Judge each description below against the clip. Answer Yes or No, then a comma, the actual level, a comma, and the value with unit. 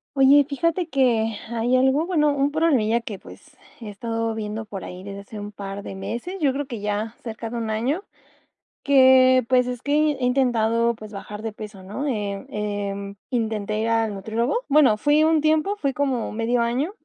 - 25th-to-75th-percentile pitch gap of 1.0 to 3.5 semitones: No, average, 4.5 semitones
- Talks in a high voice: Yes, high, 235 Hz